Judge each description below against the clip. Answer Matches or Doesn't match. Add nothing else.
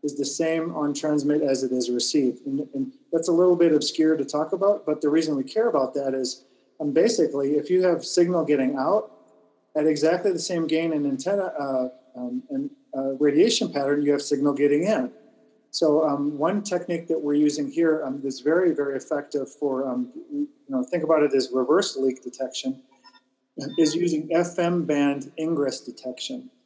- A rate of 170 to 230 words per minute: Matches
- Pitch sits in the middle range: Matches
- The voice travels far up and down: Doesn't match